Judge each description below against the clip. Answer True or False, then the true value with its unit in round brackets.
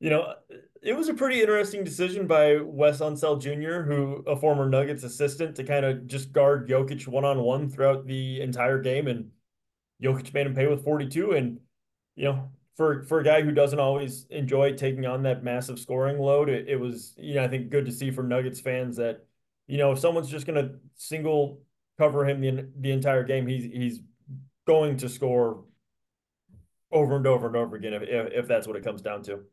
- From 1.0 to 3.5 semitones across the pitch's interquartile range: True (2.4 semitones)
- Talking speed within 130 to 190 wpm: False (205 wpm)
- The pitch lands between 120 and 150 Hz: True (135 Hz)